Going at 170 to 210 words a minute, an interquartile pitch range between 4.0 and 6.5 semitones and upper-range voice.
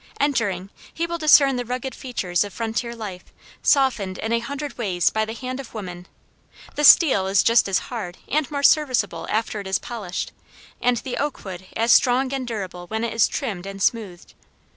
Yes: average, 190 wpm; average, 5.1 semitones; high, 230 Hz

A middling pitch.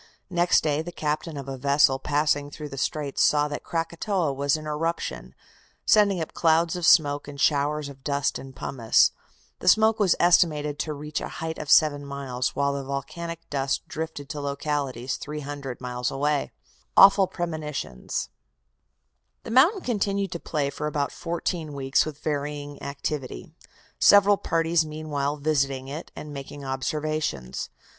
Yes: medium, 150 Hz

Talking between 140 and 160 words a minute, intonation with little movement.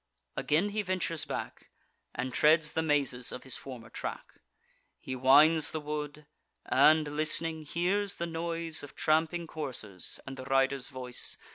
No: average, 145 wpm; average, 3.5 semitones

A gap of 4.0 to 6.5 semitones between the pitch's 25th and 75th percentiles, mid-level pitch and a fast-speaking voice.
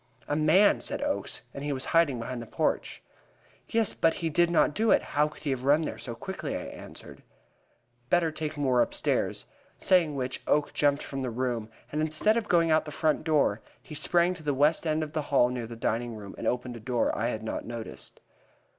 Yes: average, 4.5 semitones; medium, 145 Hz; fast, 220 wpm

